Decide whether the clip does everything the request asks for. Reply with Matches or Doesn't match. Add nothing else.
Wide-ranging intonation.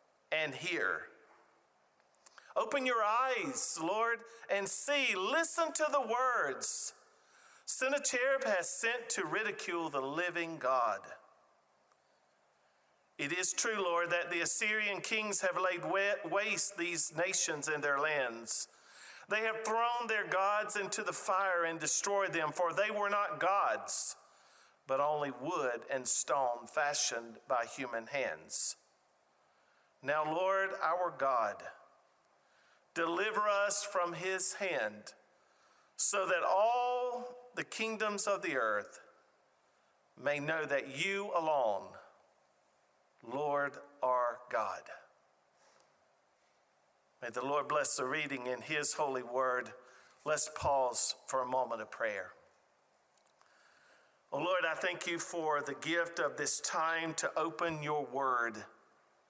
Matches